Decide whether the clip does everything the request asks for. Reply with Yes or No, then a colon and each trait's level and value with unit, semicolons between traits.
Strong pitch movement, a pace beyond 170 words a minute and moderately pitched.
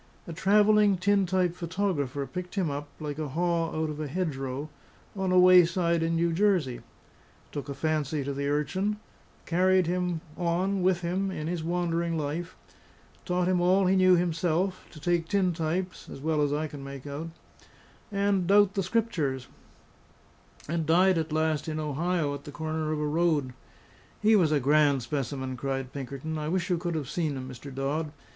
No: average, 3.7 semitones; average, 180 wpm; medium, 165 Hz